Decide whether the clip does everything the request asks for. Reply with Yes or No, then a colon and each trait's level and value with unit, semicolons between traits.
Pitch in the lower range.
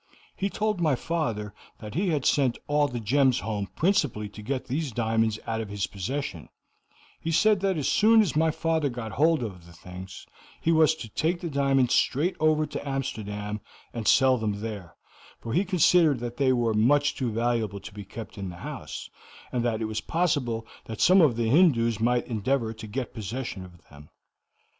Yes: low, 120 Hz